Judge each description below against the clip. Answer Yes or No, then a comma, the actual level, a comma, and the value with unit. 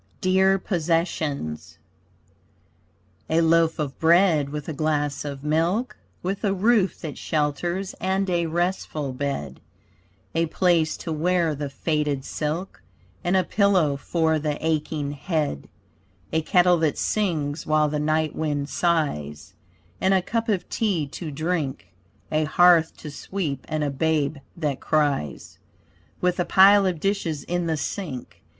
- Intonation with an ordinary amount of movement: Yes, average, 3.5 semitones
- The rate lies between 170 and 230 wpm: No, average, 140 wpm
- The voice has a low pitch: No, medium, 160 Hz